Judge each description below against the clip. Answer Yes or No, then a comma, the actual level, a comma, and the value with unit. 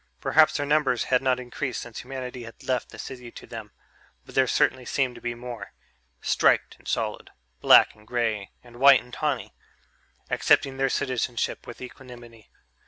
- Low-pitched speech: Yes, low, 125 Hz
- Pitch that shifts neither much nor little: No, narrow, 1.8 semitones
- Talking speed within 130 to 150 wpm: No, average, 170 wpm